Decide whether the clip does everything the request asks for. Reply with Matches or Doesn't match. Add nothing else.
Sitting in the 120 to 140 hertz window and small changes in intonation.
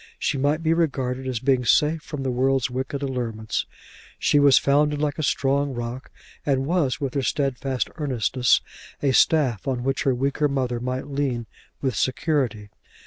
Matches